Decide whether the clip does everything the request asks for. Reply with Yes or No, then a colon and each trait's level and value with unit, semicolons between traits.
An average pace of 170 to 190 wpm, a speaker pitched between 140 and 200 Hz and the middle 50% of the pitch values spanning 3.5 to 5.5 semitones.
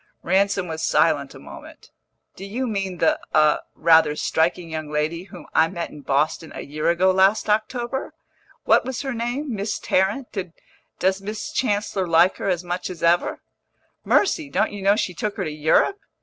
Yes: average, 175 wpm; high, 190 Hz; average, 4.6 semitones